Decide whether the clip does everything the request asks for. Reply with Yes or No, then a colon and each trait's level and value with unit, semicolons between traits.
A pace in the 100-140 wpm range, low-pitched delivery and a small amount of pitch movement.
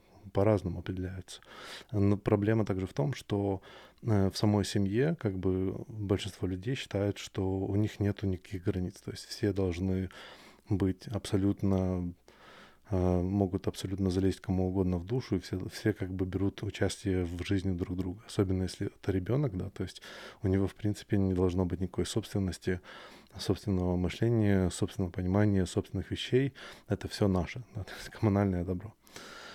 No: average, 155 wpm; very low, 95 Hz; narrow, 1.9 semitones